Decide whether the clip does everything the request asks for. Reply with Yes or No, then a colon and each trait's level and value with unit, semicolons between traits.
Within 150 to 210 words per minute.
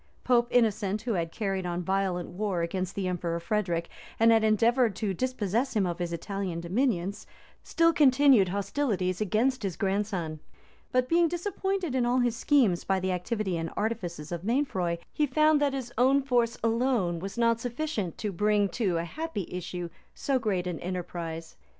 Yes: average, 170 wpm